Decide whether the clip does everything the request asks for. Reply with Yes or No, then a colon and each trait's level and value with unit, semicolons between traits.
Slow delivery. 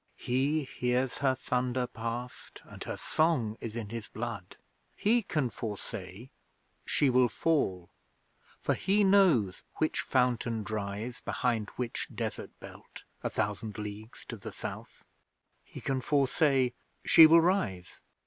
Yes: slow, 130 wpm